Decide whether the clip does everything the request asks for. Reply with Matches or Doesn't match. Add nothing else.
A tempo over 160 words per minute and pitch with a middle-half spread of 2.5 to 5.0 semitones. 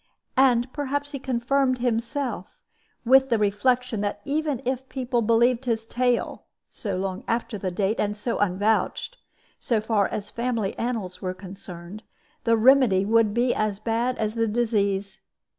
Doesn't match